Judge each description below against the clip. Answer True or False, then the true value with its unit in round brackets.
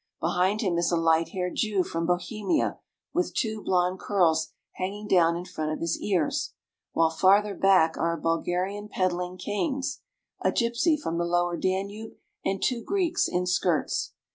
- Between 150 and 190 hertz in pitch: True (185 Hz)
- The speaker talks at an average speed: True (165 wpm)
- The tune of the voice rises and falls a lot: False (3.4 semitones)